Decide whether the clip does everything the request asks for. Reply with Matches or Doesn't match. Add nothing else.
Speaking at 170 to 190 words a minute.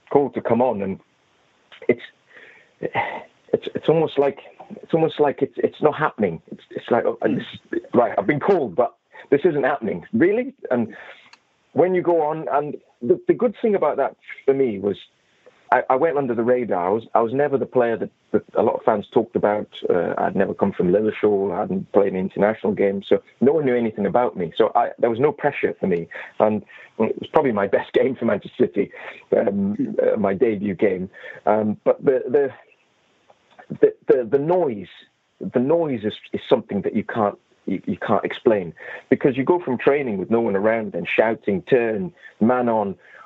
Doesn't match